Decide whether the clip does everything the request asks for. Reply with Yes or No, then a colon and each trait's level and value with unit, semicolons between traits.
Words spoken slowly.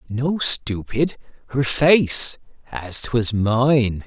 Yes: slow, 90 wpm